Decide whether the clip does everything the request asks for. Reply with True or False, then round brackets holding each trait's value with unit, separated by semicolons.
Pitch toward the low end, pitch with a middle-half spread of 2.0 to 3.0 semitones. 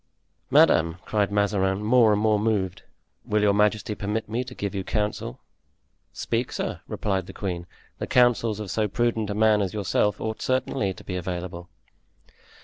True (105 Hz; 2.4 semitones)